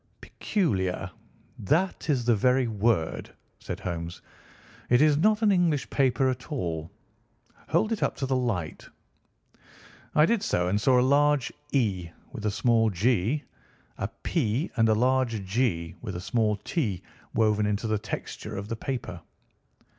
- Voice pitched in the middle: No, low, 115 Hz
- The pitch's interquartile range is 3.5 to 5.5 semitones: Yes, average, 4.9 semitones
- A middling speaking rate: Yes, average, 150 wpm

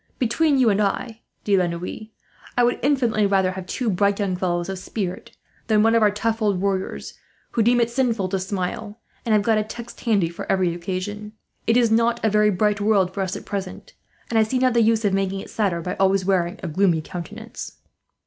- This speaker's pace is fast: Yes, fast, 220 wpm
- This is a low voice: No, high, 205 Hz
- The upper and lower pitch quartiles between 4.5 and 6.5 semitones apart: No, average, 3.2 semitones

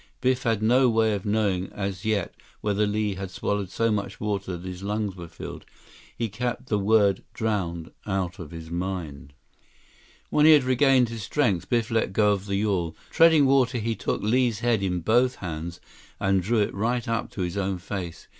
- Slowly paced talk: No, average, 190 wpm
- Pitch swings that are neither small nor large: Yes, average, 3.6 semitones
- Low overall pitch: Yes, low, 105 Hz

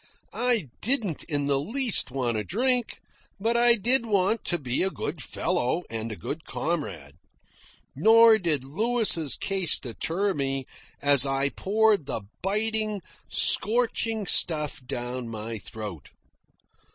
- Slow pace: Yes, slow, 130 wpm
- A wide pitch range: Yes, wide, 8.6 semitones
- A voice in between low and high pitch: Yes, medium, 170 Hz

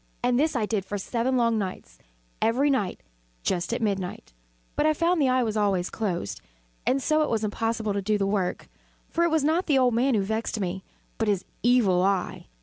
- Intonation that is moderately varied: Yes, average, 4.6 semitones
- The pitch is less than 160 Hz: No, high, 225 Hz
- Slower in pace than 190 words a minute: No, fast, 205 wpm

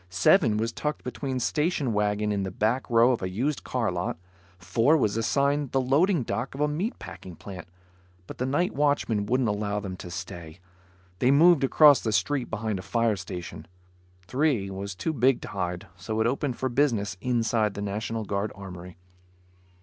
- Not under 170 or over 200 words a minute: Yes, average, 180 wpm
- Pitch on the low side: Yes, low, 115 Hz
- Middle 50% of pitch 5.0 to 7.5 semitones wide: Yes, average, 5.3 semitones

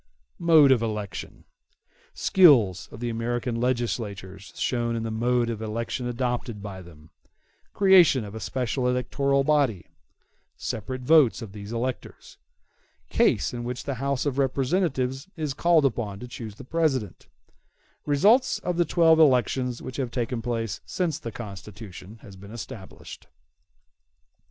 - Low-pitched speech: Yes, low, 120 Hz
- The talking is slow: Yes, slow, 130 wpm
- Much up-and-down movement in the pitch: No, average, 3.9 semitones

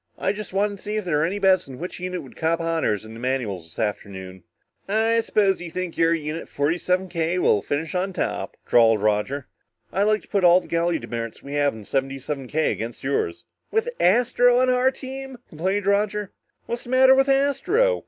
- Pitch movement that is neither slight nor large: No, wide, 7.3 semitones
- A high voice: No, medium, 175 Hz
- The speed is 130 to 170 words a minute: No, fast, 205 wpm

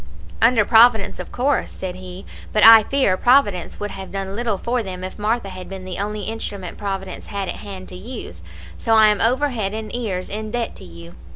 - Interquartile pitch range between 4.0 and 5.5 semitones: No, average, 3.3 semitones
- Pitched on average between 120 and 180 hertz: No, high, 205 Hz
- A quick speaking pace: Yes, fast, 210 wpm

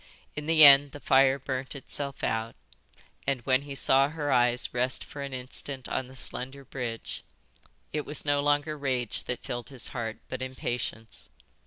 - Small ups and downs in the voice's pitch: Yes, narrow, 2.3 semitones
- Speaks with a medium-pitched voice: No, low, 130 Hz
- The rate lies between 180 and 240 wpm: No, average, 170 wpm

